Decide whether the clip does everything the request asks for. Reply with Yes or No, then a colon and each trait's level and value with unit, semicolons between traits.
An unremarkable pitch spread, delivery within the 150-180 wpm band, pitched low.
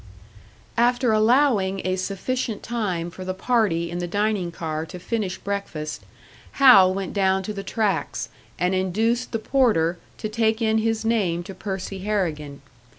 No: average, 3.6 semitones; average, 155 wpm; high, 195 Hz